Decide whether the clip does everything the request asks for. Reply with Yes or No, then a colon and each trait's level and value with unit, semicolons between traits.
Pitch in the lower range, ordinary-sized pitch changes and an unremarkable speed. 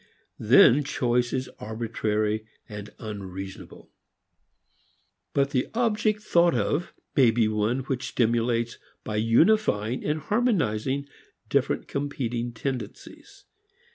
No: low, 120 Hz; average, 4.6 semitones; slow, 90 wpm